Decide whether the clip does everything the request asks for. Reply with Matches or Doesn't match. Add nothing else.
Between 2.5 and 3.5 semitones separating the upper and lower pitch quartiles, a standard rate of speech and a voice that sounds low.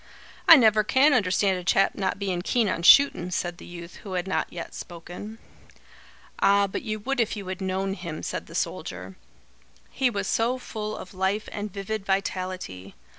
Doesn't match